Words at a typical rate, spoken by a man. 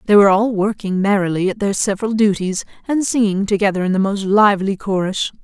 No: average, 190 wpm; female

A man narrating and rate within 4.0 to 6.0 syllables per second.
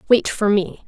No: female; 4.5 syllables/s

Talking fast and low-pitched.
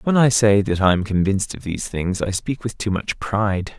Yes: fast, 255 wpm; low, 100 Hz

